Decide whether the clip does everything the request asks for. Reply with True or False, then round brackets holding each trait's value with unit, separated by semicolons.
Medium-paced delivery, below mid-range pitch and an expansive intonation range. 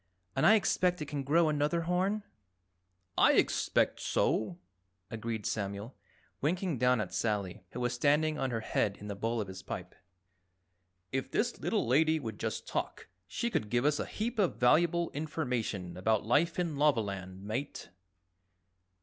True (160 wpm; 130 Hz; 6.8 semitones)